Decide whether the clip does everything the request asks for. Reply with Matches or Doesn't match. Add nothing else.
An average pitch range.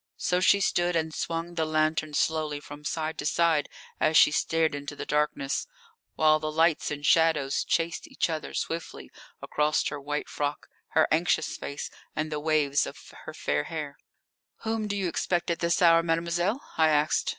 Doesn't match